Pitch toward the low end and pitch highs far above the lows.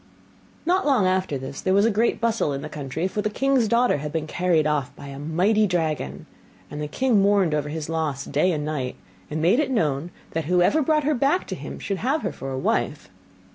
No: medium, 170 Hz; wide, 6.9 semitones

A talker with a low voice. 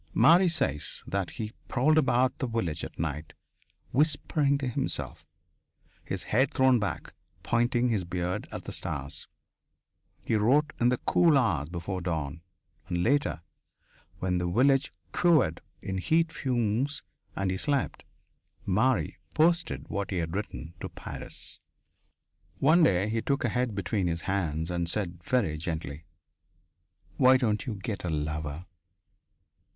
Yes: low, 105 Hz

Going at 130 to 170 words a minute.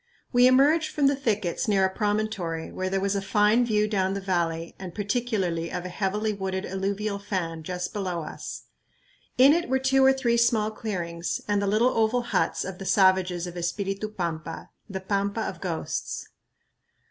No: average, 180 wpm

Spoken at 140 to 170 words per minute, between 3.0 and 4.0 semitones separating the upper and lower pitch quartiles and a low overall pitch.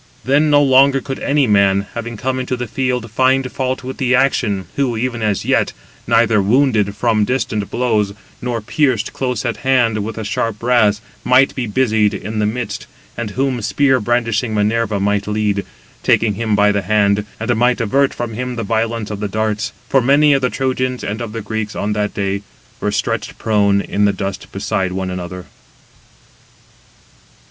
No: average, 185 wpm; average, 3.5 semitones; low, 115 Hz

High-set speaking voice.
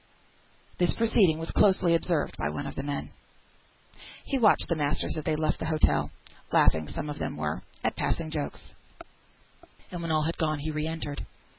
No: medium, 155 Hz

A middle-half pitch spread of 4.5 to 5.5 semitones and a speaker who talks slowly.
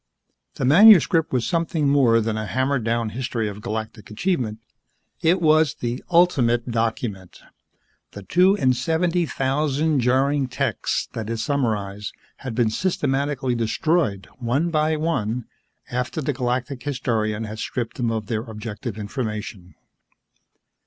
Yes: average, 4.9 semitones; slow, 130 wpm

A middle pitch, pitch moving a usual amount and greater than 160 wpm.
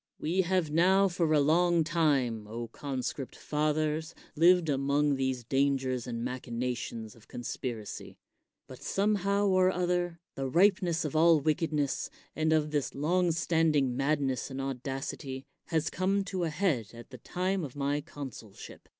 No: medium, 150 Hz; average, 4.6 semitones; average, 150 wpm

